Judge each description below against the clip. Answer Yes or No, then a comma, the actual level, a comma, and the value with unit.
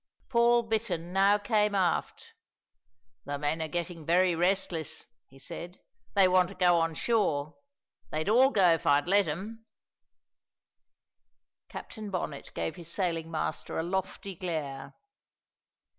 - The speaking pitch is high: No, medium, 180 Hz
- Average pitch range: Yes, average, 3.8 semitones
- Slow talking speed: Yes, slow, 130 wpm